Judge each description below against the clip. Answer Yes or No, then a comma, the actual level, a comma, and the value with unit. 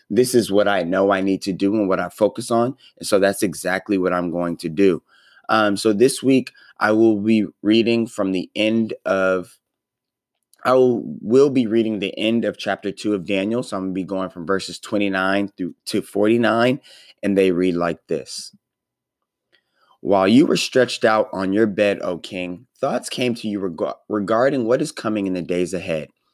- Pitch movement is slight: No, average, 3.1 semitones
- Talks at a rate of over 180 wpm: Yes, average, 200 wpm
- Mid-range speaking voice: No, low, 100 Hz